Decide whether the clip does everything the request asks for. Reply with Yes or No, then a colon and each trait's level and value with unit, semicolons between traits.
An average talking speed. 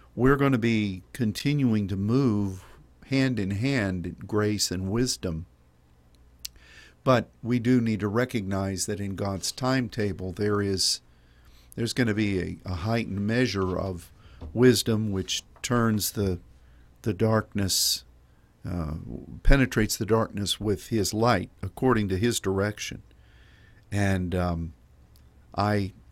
No: slow, 125 wpm